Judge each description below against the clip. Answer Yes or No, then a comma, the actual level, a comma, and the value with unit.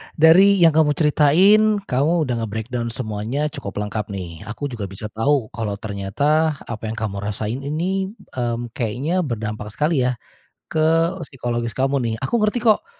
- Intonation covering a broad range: Yes, wide, 6.3 semitones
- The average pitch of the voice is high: No, low, 130 Hz